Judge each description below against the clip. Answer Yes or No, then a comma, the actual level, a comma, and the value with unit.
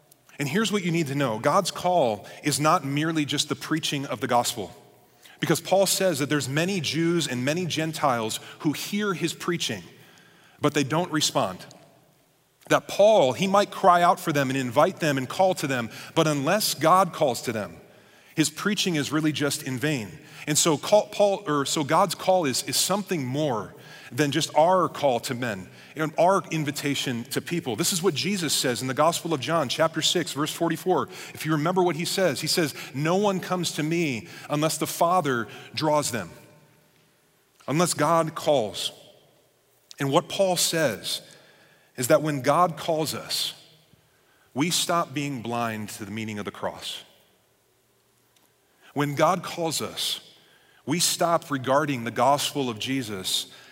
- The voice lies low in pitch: No, medium, 155 Hz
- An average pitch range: Yes, average, 3.6 semitones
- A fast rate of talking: No, average, 170 wpm